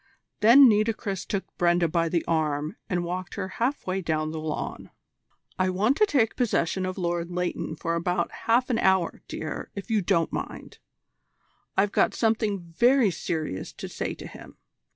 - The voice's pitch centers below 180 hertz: No, medium, 185 Hz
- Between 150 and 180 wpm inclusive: Yes, average, 170 wpm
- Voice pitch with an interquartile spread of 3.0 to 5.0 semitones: Yes, average, 4.4 semitones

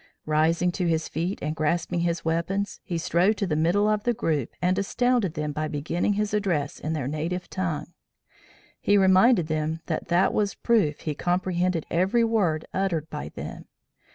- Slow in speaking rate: No, average, 175 wpm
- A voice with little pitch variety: No, average, 3.8 semitones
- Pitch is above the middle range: No, medium, 175 Hz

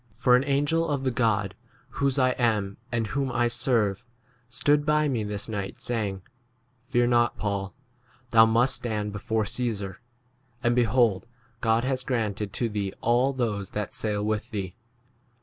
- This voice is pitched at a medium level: No, low, 115 Hz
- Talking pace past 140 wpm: Yes, average, 165 wpm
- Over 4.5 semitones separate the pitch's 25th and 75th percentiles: No, average, 3.4 semitones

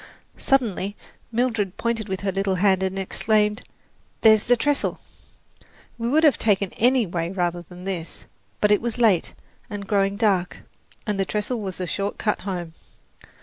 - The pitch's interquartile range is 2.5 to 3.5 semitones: Yes, average, 3.0 semitones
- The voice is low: No, high, 200 Hz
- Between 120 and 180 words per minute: Yes, average, 160 wpm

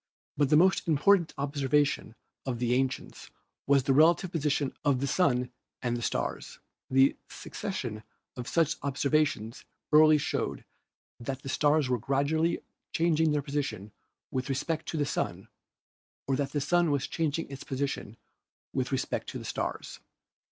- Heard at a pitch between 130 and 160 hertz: Yes, medium, 140 Hz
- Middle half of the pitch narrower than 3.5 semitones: Yes, average, 2.9 semitones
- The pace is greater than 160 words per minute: No, average, 150 wpm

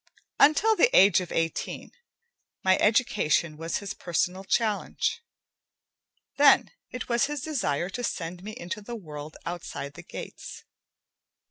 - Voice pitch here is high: Yes, high, 195 Hz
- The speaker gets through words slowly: Yes, slow, 130 wpm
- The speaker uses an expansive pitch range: Yes, wide, 6.4 semitones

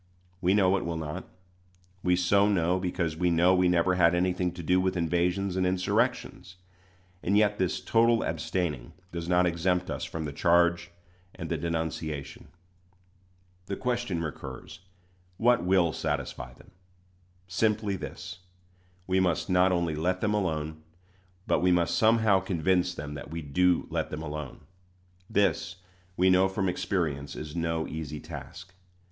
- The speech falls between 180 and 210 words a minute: No, average, 150 wpm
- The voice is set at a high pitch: No, very low, 90 Hz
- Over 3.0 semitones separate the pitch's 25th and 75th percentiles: No, narrow, 2.5 semitones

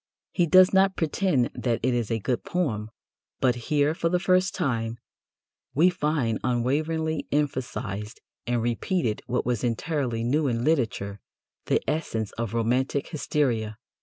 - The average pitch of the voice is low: Yes, low, 130 Hz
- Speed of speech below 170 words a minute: Yes, average, 140 wpm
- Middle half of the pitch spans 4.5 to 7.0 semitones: Yes, wide, 5.4 semitones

